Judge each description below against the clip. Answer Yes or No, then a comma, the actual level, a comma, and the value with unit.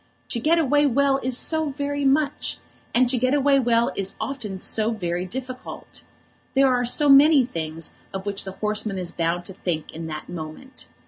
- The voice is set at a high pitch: Yes, high, 245 Hz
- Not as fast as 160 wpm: No, average, 185 wpm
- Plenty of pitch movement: Yes, wide, 6.6 semitones